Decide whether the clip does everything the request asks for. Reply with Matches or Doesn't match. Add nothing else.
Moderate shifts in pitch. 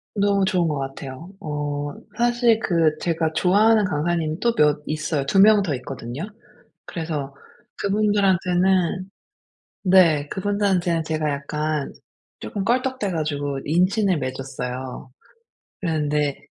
Matches